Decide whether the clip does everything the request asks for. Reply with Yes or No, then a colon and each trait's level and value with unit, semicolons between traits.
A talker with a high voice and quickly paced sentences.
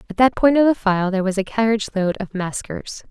Yes: high, 210 Hz; fast, 250 wpm